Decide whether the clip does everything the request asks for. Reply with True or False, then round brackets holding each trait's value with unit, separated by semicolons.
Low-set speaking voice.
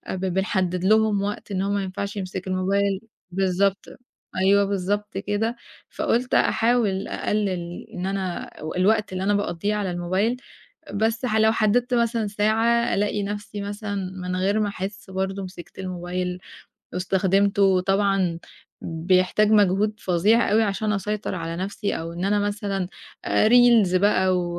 False (200 Hz)